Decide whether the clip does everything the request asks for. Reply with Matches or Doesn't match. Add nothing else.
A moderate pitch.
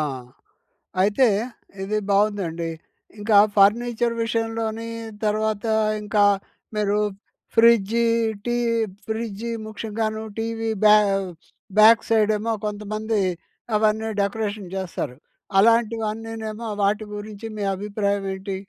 Doesn't match